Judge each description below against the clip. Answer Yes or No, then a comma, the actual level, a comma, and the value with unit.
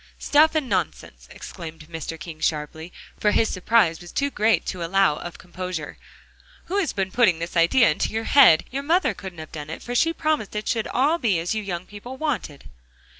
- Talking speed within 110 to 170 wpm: No, average, 200 wpm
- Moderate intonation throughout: No, wide, 7.0 semitones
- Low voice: No, high, 195 Hz